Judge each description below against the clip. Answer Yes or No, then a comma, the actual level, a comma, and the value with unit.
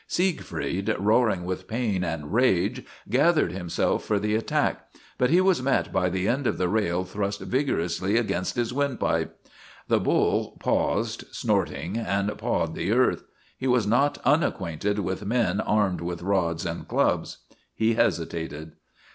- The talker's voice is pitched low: Yes, low, 100 Hz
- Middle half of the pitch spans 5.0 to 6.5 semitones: Yes, average, 5.3 semitones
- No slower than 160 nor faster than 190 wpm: No, average, 145 wpm